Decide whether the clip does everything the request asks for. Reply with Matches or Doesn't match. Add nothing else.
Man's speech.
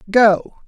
Doesn't match